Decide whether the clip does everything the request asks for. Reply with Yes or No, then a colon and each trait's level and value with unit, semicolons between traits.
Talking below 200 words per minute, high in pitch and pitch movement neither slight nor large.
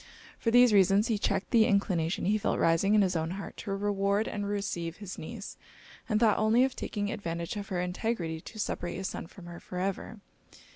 No: fast, 205 wpm; high, 200 Hz; average, 3.1 semitones